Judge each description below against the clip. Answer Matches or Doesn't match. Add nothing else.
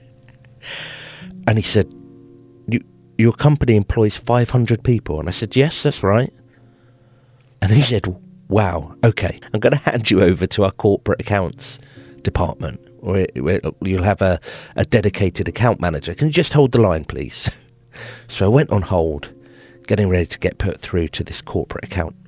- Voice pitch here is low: Matches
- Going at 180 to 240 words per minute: Doesn't match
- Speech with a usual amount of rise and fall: Doesn't match